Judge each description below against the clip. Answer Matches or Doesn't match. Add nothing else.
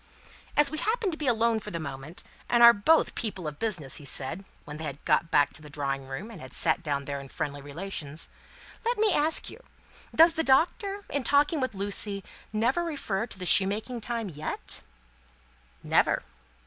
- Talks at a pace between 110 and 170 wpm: Doesn't match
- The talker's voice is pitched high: Matches